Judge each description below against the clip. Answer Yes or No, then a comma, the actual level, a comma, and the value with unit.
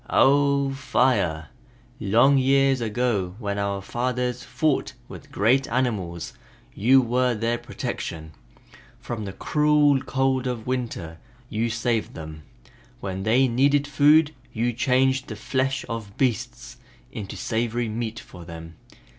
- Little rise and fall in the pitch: No, average, 4.1 semitones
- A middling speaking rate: No, slow, 125 wpm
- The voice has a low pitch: Yes, low, 120 Hz